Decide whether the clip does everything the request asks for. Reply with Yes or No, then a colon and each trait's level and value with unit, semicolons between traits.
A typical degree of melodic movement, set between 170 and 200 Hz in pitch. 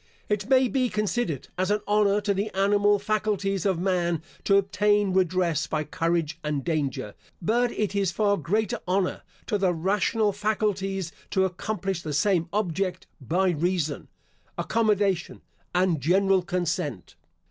Yes: average, 3.2 semitones; high, 190 Hz